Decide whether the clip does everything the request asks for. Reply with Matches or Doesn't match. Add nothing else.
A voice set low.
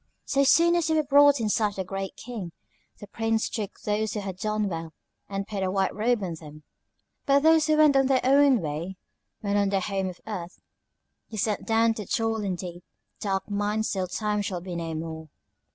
Doesn't match